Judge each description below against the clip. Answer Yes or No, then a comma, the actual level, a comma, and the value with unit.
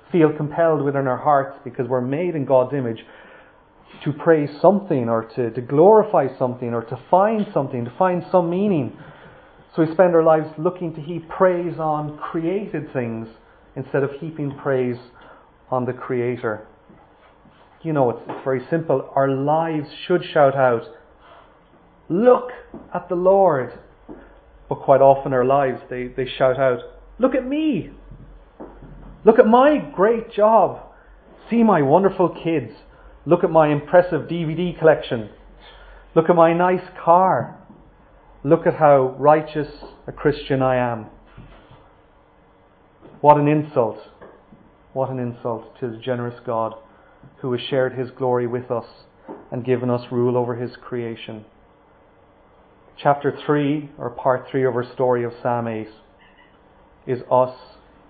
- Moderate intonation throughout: Yes, average, 4.8 semitones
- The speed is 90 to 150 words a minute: Yes, average, 145 wpm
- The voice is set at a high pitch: No, medium, 140 Hz